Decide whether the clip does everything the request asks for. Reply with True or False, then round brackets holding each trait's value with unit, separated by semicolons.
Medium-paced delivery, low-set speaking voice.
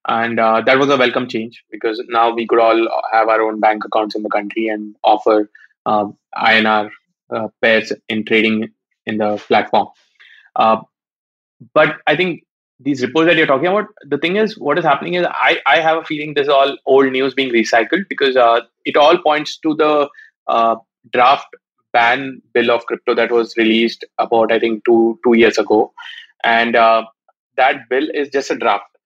True (190 wpm; 115 Hz)